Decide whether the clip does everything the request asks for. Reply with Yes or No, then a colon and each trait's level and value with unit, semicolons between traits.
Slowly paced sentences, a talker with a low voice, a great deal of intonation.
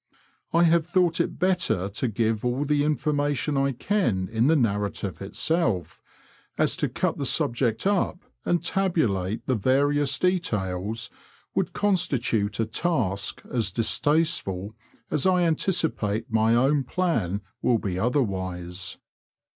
Yes: slow, 130 wpm; low, 125 Hz; wide, 7.8 semitones